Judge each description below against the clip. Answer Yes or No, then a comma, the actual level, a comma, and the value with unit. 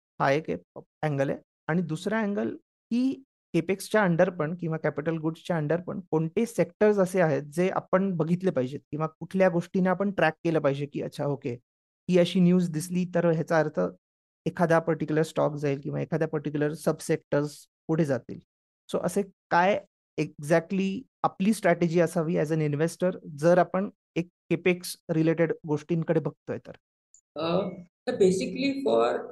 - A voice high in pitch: No, medium, 165 Hz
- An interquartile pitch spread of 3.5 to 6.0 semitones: No, average, 3.0 semitones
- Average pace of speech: No, fast, 145 wpm